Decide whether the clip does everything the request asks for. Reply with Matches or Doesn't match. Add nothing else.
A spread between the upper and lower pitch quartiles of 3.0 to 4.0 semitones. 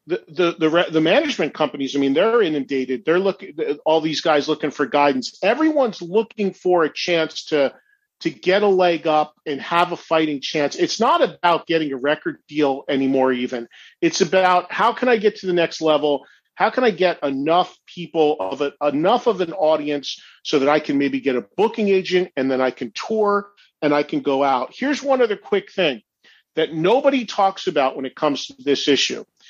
Doesn't match